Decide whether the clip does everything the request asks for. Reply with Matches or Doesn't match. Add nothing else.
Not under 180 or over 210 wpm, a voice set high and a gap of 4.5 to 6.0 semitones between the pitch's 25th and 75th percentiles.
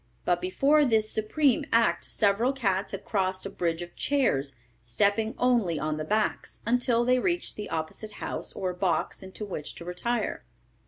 Doesn't match